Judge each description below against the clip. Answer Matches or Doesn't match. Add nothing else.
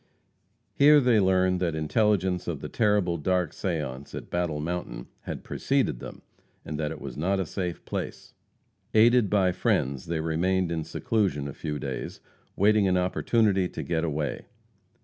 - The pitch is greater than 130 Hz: Doesn't match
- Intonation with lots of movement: Doesn't match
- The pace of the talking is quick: Doesn't match